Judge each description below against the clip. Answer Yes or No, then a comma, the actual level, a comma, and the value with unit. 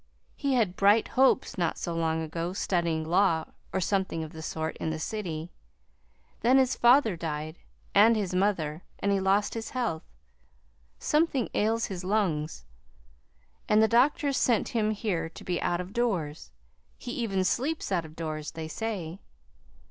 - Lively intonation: Yes, wide, 5.7 semitones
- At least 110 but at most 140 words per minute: No, average, 160 wpm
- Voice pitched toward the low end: No, high, 190 Hz